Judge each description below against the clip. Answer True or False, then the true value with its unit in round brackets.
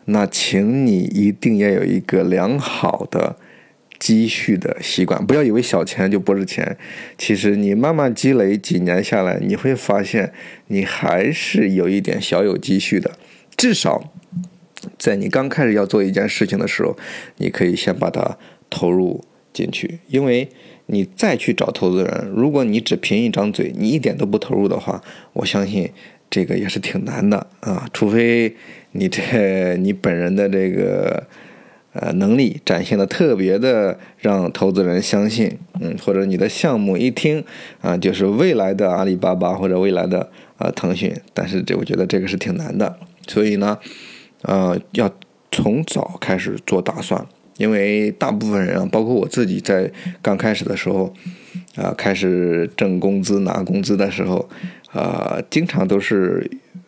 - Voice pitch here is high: False (100 Hz)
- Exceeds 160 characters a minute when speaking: True (245 characters per minute)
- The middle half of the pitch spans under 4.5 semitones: False (5.6 semitones)